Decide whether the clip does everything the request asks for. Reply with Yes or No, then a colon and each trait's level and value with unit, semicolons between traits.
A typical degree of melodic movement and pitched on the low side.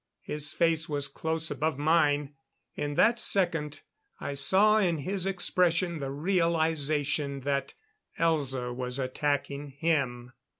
No: average, 3.2 semitones; medium, 150 Hz